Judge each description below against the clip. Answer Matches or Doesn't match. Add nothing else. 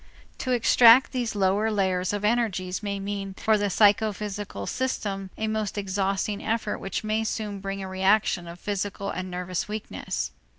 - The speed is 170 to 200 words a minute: Doesn't match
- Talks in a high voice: Matches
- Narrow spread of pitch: Matches